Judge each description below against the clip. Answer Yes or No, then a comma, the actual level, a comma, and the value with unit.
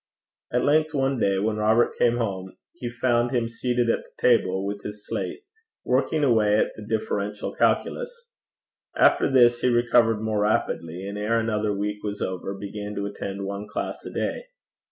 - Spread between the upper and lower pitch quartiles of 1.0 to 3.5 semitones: Yes, average, 3.1 semitones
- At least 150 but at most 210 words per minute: Yes, average, 175 wpm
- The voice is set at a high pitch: No, low, 110 Hz